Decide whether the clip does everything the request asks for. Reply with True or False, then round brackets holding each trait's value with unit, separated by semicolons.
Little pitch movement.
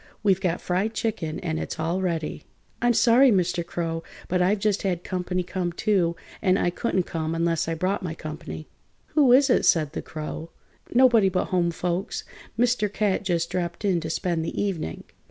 False (3.4 semitones)